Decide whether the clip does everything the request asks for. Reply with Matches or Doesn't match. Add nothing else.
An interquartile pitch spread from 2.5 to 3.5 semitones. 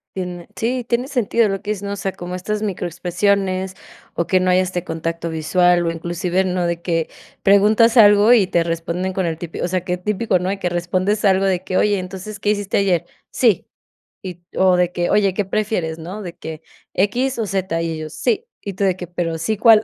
Matches